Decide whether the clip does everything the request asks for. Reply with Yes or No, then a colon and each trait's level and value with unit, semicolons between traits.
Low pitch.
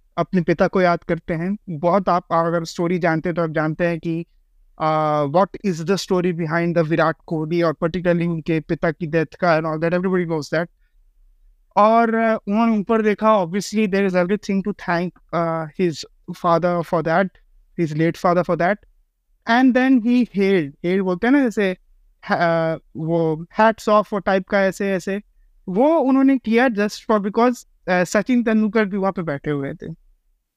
No: medium, 180 Hz